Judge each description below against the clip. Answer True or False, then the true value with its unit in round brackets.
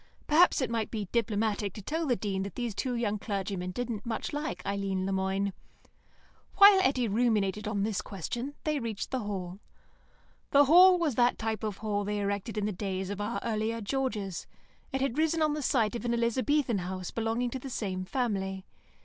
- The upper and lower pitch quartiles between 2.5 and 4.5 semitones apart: True (4.1 semitones)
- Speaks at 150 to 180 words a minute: False (190 wpm)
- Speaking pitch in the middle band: False (220 Hz)